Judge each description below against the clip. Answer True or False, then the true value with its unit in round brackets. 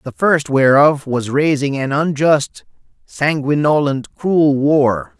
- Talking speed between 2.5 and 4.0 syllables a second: True (3.5 syllables/s)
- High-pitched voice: False (145 Hz)